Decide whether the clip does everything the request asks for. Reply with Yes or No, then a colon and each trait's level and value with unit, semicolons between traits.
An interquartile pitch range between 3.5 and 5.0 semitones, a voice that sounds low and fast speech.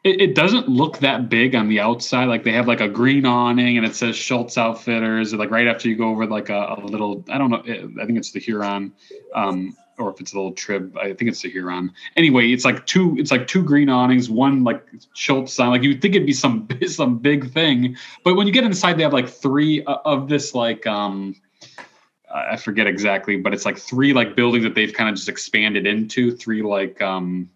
Yes: average, 4.3 semitones; low, 120 Hz; fast, 235 wpm